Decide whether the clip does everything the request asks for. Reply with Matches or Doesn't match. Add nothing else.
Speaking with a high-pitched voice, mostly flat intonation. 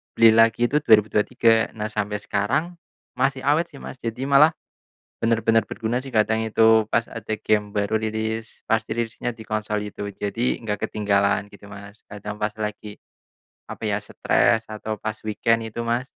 Doesn't match